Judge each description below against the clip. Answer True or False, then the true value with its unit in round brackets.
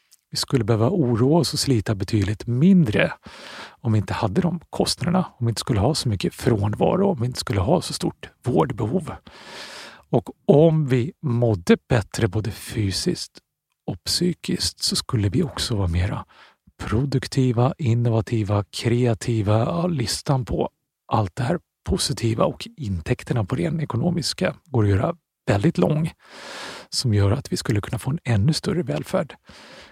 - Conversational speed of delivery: True (155 wpm)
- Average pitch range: False (5.7 semitones)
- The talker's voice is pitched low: True (120 Hz)